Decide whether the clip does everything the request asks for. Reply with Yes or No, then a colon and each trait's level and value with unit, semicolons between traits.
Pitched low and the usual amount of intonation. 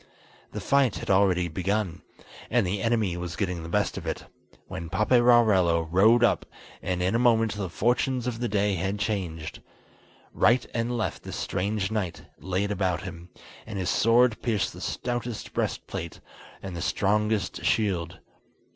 Yes: low, 100 Hz; average, 4.2 semitones